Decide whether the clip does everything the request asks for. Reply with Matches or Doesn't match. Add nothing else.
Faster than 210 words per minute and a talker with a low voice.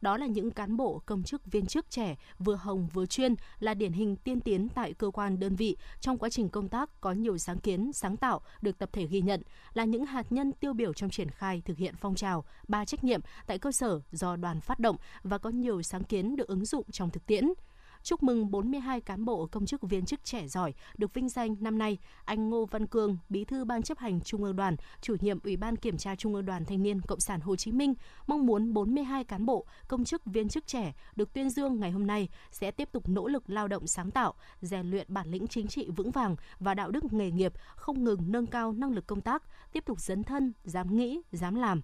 Doesn't match